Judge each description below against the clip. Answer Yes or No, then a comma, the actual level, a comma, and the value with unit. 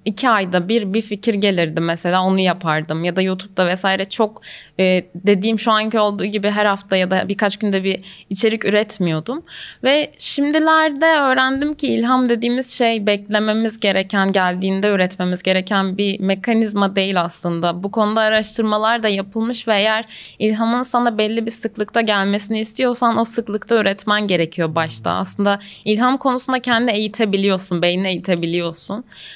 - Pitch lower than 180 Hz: No, high, 210 Hz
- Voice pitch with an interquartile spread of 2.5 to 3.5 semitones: Yes, average, 3.1 semitones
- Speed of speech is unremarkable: No, fast, 145 wpm